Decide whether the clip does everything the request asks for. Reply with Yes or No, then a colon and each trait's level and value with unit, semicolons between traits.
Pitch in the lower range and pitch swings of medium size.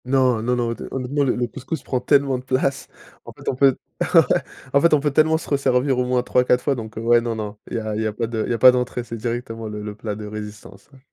Yes: low, 125 Hz; average, 3.0 semitones